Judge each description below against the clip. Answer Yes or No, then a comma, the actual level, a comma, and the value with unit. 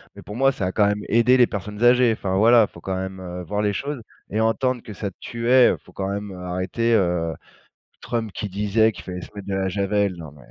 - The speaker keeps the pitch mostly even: No, average, 3.6 semitones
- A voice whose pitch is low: Yes, low, 105 Hz